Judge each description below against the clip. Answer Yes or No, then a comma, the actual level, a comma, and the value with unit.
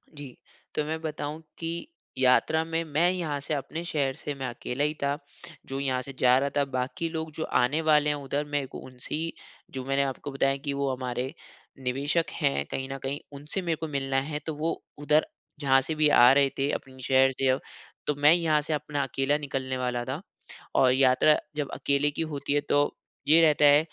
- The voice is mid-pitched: Yes, medium, 145 Hz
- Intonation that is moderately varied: No, narrow, 2.3 semitones